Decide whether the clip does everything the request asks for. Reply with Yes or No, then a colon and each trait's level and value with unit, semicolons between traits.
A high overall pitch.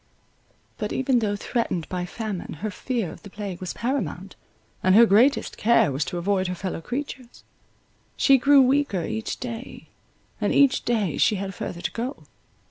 Yes: high, 215 Hz